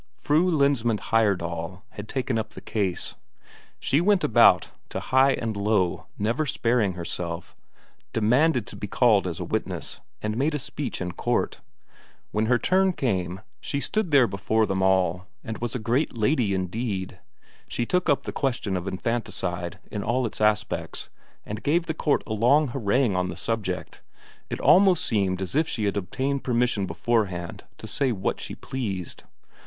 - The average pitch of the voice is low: Yes, low, 110 Hz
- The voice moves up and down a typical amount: No, wide, 5.8 semitones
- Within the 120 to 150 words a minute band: No, average, 170 wpm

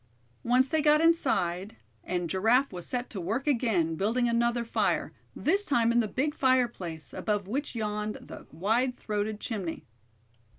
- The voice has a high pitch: Yes, high, 230 Hz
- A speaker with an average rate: Yes, average, 155 wpm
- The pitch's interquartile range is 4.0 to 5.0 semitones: Yes, average, 4.4 semitones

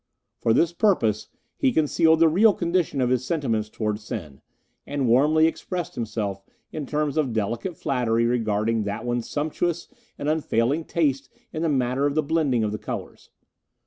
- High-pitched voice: No, low, 135 Hz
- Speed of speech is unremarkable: Yes, average, 165 wpm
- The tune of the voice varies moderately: No, wide, 5.8 semitones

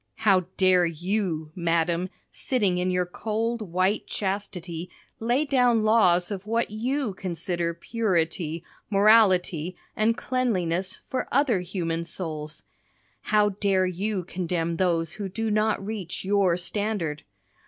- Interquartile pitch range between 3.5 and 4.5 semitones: Yes, average, 3.9 semitones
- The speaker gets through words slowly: Yes, slow, 120 wpm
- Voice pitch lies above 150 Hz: Yes, medium, 185 Hz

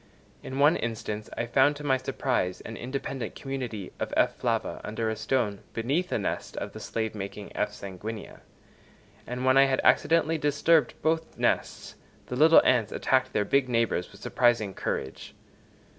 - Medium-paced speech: Yes, average, 165 wpm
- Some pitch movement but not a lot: Yes, average, 4.0 semitones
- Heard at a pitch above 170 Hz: No, low, 125 Hz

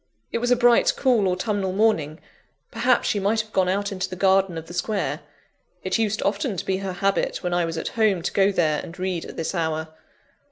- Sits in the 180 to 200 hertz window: Yes, high, 190 Hz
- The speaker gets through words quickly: Yes, fast, 220 wpm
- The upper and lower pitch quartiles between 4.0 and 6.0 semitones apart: No, average, 3.2 semitones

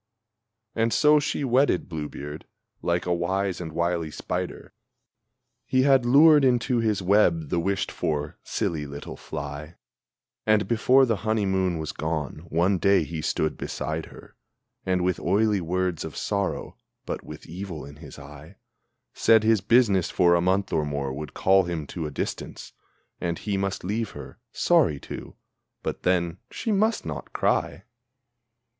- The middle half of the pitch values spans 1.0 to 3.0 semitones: No, average, 5.3 semitones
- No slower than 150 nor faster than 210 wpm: Yes, average, 155 wpm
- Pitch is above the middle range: No, very low, 90 Hz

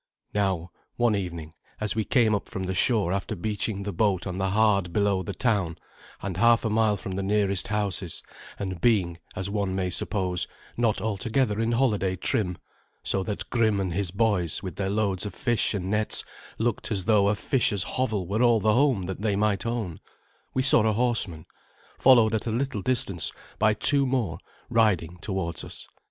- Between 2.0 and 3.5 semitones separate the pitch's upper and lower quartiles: Yes, average, 3.1 semitones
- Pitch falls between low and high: No, low, 100 Hz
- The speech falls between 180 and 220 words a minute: Yes, average, 185 wpm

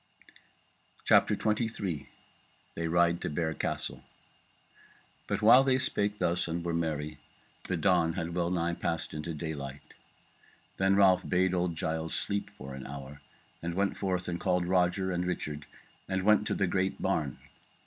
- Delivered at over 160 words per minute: No, average, 150 wpm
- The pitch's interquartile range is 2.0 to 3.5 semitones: Yes, average, 2.8 semitones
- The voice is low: Yes, very low, 85 Hz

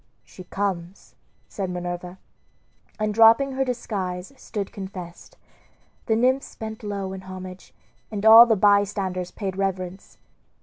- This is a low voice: No, high, 195 Hz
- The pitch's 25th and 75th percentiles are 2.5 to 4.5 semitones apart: Yes, average, 3.0 semitones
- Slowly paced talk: Yes, slow, 125 wpm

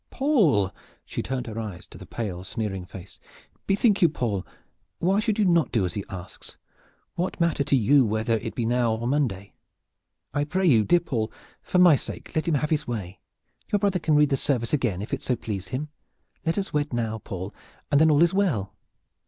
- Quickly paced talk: Yes, fast, 210 wpm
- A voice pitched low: Yes, low, 130 Hz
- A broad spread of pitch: Yes, wide, 7.4 semitones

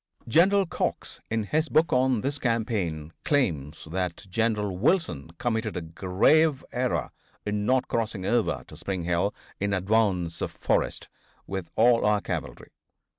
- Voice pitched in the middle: No, low, 105 Hz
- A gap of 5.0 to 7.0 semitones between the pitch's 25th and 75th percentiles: Yes, wide, 5.6 semitones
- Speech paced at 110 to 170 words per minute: Yes, average, 140 wpm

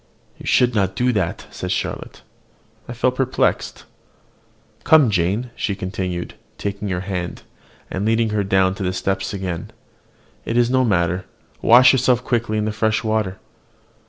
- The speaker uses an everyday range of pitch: Yes, average, 4.1 semitones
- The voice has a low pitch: Yes, low, 105 Hz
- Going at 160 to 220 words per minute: No, average, 150 wpm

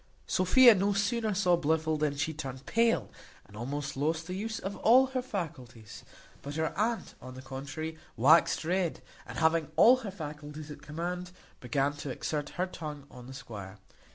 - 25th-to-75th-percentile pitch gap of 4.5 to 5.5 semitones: Yes, average, 4.9 semitones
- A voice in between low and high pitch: Yes, medium, 160 Hz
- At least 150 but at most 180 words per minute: Yes, average, 175 wpm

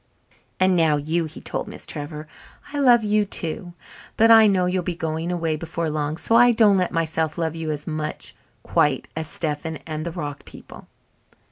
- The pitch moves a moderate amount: Yes, average, 3.0 semitones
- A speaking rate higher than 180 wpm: Yes, average, 190 wpm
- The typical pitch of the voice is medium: Yes, medium, 165 Hz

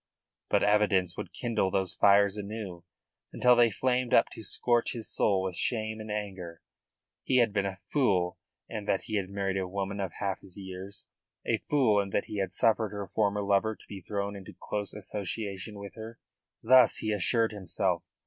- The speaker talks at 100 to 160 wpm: No, average, 185 wpm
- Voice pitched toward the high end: No, low, 100 Hz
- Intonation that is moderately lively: No, narrow, 2.3 semitones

